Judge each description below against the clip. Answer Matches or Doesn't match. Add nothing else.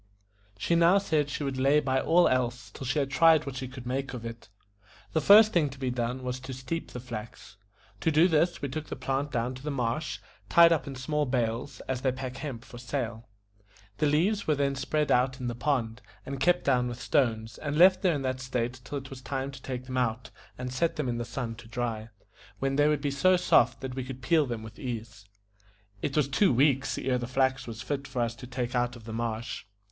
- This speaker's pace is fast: Matches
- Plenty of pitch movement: Doesn't match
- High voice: Doesn't match